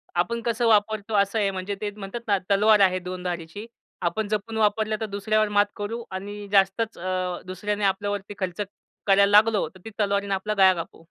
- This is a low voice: No, high, 205 Hz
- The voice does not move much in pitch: Yes, narrow, 2.1 semitones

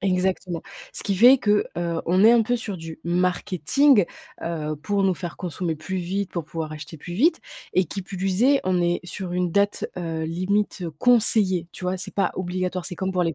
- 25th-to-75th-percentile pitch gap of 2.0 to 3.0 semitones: Yes, average, 2.7 semitones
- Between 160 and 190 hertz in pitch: Yes, medium, 185 Hz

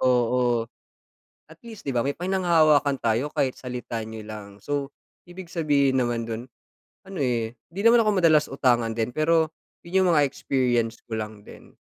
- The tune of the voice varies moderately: No, wide, 5.8 semitones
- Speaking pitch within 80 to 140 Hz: Yes, low, 135 Hz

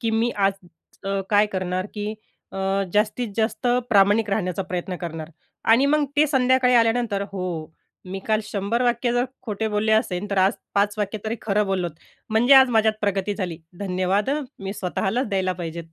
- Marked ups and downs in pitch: No, average, 3.2 semitones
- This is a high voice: Yes, high, 205 Hz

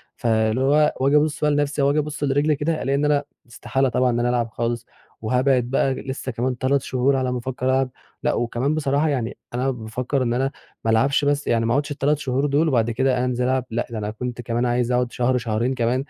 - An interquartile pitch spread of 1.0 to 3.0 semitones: Yes, average, 2.7 semitones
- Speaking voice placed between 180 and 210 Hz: No, low, 130 Hz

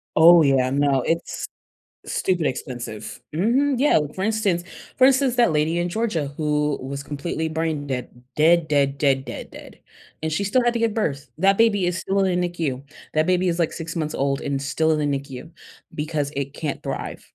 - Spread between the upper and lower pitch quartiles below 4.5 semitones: No, average, 4.8 semitones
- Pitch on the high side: No, medium, 160 Hz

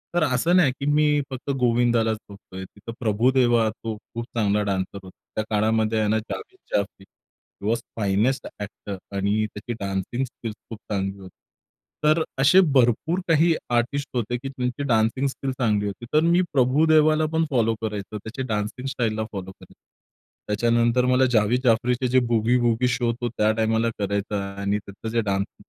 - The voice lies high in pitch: No, low, 115 Hz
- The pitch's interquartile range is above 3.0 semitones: Yes, average, 3.6 semitones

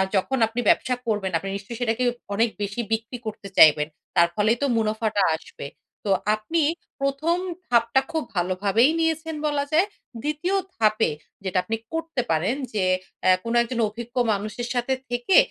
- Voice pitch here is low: No, high, 230 Hz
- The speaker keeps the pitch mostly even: No, average, 4.7 semitones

